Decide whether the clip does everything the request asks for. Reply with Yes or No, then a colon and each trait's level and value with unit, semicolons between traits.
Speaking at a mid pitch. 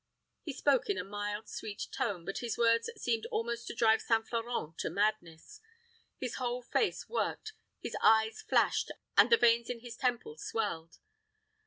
No: high, 230 Hz